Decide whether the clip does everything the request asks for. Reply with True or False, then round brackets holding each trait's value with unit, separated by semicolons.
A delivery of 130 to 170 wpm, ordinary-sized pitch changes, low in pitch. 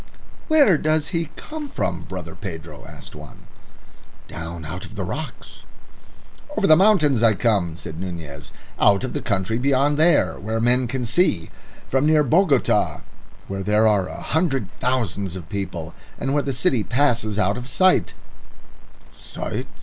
False (155 wpm; 7.7 semitones; 115 Hz)